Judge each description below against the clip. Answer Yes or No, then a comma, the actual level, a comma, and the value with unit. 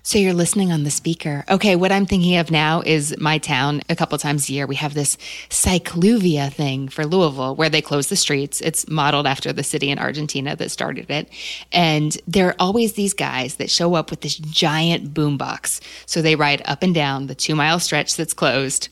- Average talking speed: No, fast, 215 wpm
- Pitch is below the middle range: No, medium, 155 Hz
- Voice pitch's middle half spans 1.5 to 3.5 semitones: Yes, average, 3.1 semitones